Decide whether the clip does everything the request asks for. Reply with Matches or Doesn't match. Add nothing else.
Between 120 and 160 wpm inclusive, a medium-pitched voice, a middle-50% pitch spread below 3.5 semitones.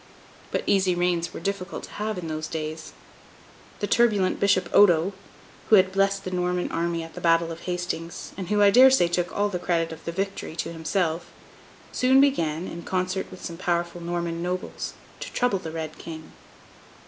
Doesn't match